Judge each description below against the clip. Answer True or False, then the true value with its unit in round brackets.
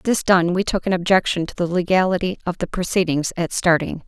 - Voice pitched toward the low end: False (180 Hz)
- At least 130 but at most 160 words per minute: False (205 wpm)